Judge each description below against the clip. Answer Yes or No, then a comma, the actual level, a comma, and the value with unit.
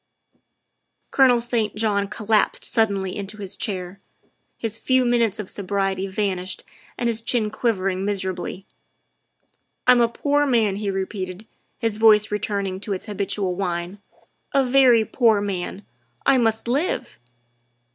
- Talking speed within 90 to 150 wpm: Yes, slow, 135 wpm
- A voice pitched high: Yes, high, 210 Hz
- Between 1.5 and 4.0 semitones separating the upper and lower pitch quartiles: Yes, average, 3.2 semitones